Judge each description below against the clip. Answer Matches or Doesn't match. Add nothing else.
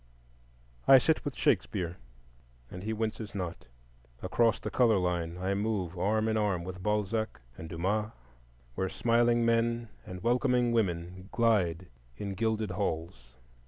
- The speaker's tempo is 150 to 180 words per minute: Doesn't match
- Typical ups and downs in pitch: Matches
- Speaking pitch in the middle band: Doesn't match